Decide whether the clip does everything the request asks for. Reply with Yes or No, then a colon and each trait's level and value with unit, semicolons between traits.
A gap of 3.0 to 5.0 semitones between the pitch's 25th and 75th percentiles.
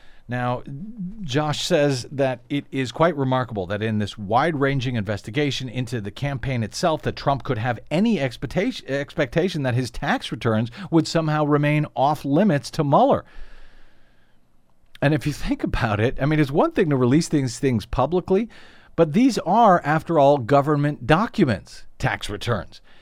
Yes: average, 4.3 semitones